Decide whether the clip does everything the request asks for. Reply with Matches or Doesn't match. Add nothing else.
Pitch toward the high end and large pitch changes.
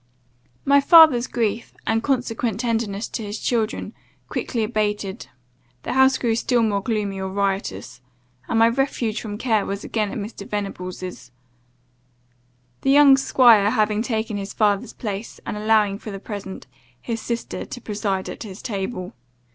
Doesn't match